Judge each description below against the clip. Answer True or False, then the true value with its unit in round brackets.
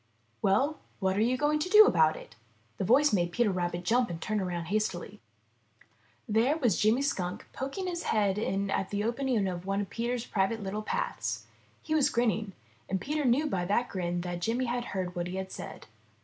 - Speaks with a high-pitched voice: True (215 Hz)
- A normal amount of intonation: True (5.0 semitones)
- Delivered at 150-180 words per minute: False (195 wpm)